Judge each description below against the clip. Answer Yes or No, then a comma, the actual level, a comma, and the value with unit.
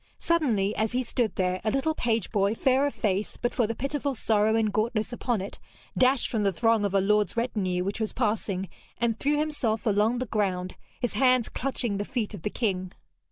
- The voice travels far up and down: No, average, 3.5 semitones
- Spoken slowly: No, fast, 205 wpm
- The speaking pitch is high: Yes, high, 220 Hz